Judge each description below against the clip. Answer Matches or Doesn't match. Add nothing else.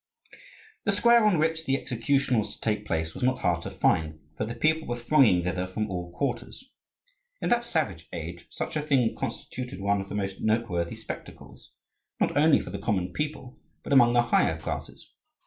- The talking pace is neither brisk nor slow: Matches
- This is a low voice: Matches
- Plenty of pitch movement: Matches